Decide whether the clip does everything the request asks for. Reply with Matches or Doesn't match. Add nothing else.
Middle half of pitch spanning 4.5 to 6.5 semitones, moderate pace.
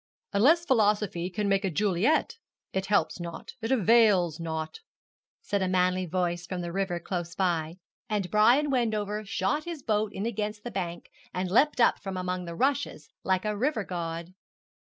Doesn't match